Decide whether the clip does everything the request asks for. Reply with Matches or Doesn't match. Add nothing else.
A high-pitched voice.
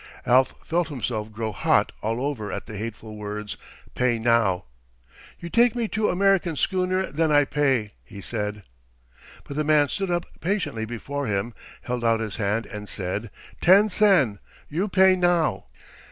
Doesn't match